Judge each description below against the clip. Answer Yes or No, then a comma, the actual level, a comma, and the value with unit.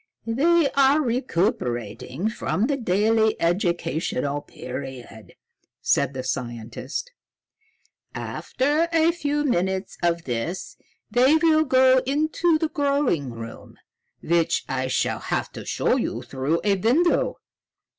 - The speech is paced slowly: Yes, slow, 115 wpm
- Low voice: No, high, 205 Hz